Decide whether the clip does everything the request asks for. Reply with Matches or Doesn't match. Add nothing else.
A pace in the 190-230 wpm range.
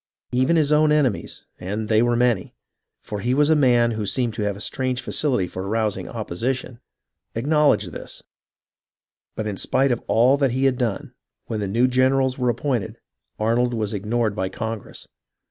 Doesn't match